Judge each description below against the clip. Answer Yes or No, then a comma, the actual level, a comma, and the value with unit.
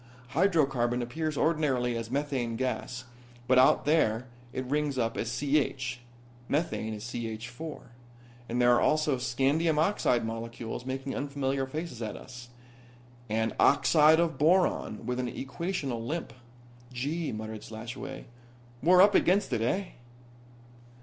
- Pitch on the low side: Yes, low, 130 Hz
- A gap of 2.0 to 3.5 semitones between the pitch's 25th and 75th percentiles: No, average, 4.3 semitones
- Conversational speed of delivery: No, slow, 130 wpm